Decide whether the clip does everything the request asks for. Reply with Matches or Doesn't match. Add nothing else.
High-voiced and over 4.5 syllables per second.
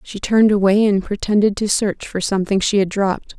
Matches